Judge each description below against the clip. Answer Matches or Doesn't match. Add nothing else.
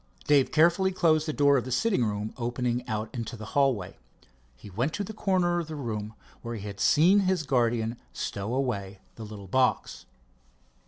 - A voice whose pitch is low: Matches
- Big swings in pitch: Matches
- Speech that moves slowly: Doesn't match